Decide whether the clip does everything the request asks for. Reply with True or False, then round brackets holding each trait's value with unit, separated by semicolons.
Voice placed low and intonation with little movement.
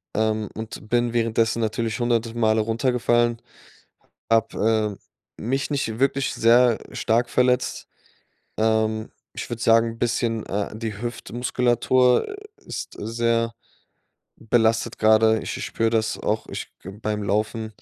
True (115 Hz; 1.4 semitones)